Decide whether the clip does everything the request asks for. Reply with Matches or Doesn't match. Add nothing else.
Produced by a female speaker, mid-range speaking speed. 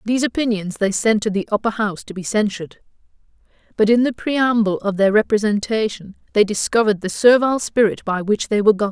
Matches